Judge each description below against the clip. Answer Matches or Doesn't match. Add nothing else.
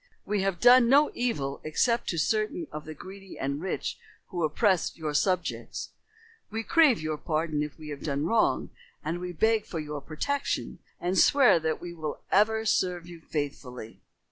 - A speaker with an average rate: Matches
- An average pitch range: Doesn't match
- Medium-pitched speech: Matches